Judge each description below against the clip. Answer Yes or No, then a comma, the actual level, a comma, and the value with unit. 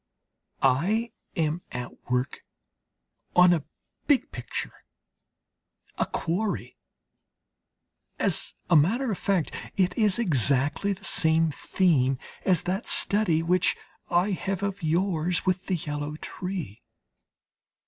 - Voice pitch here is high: No, medium, 175 Hz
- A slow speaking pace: Yes, slow, 110 wpm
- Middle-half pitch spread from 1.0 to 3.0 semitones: No, average, 4.2 semitones